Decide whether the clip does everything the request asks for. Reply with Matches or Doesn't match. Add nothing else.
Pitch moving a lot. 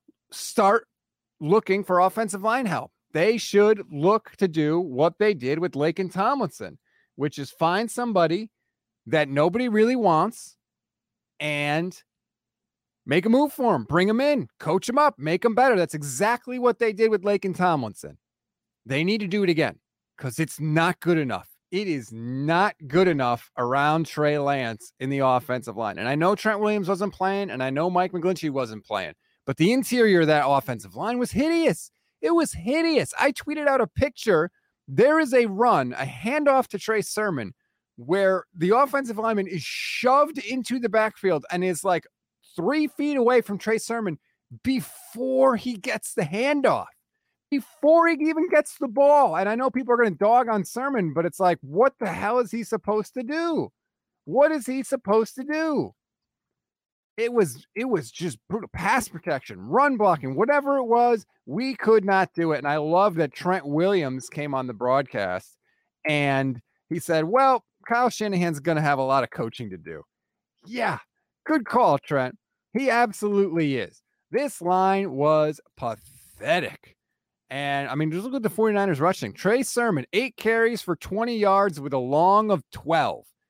Matches